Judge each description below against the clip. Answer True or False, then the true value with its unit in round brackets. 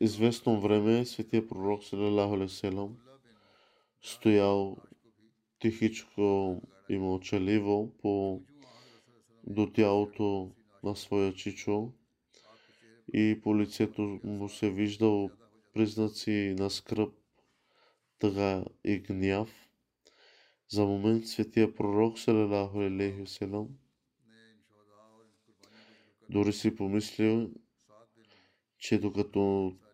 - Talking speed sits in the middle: False (75 wpm)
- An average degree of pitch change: False (1.7 semitones)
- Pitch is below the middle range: True (105 Hz)